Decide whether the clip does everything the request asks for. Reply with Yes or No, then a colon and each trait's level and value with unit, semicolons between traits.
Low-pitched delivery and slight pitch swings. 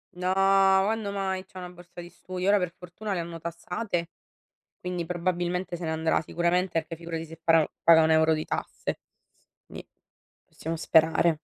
No: medium, 175 Hz; narrow, 2.2 semitones